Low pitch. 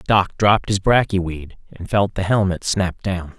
Yes: very low, 95 Hz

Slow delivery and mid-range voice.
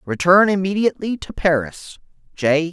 Yes: slow, 90 wpm; medium, 175 Hz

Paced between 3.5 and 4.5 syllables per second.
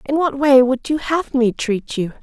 Yes: 4.4 syllables/s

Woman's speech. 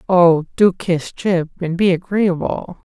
No: male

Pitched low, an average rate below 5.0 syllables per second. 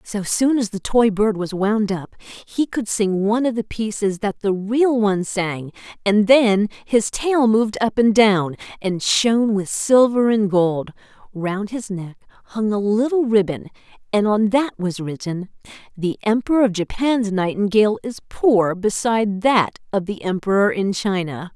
No: high, 210 Hz; 4.4 syllables/s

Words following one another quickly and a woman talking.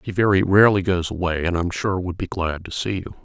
No: fast, 280 wpm; male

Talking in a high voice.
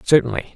No: low, 115 Hz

